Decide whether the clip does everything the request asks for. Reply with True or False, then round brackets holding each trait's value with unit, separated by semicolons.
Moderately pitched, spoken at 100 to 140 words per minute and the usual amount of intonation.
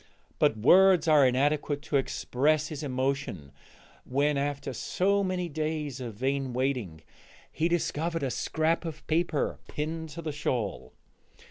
True (145 Hz; 135 wpm; 3.4 semitones)